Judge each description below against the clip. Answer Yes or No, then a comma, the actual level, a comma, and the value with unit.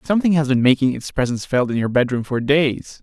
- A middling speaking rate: No, fast, 260 wpm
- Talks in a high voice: No, low, 135 Hz